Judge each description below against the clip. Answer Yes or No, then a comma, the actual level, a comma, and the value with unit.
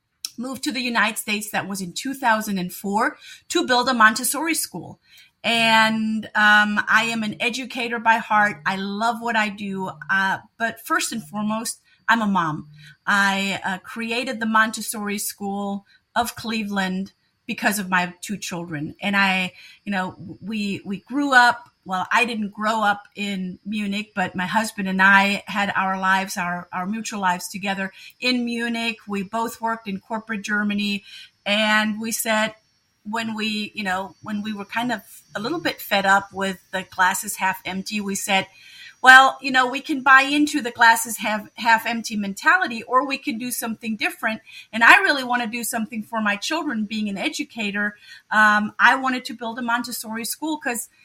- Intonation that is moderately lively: Yes, average, 3.1 semitones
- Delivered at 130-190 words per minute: Yes, average, 175 wpm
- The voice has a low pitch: No, high, 215 Hz